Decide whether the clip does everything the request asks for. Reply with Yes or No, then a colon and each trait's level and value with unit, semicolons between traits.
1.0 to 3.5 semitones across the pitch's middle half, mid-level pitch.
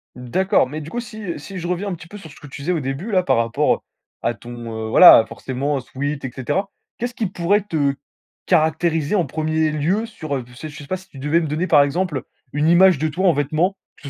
No: average, 4.8 semitones; medium, 155 Hz